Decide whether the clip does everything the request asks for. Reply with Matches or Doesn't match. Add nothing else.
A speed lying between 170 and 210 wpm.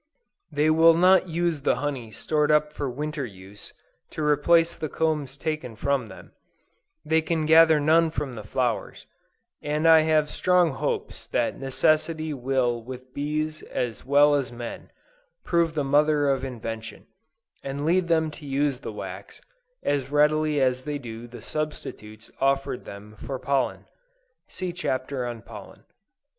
Doesn't match